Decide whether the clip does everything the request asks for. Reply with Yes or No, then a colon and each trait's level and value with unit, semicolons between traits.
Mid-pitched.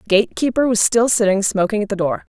No: high, 210 Hz